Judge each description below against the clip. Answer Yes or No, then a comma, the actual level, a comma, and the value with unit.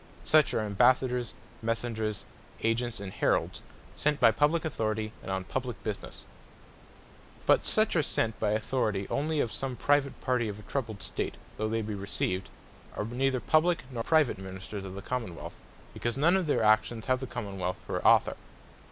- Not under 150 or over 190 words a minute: Yes, average, 180 wpm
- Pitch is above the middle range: No, low, 115 Hz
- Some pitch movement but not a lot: Yes, average, 4.1 semitones